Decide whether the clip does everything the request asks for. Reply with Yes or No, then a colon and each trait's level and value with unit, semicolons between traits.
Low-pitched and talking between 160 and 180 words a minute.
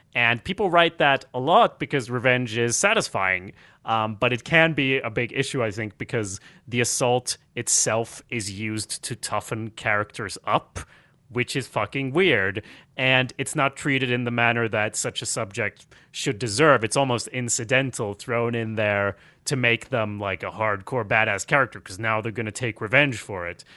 Yes: low, 120 Hz; average, 175 wpm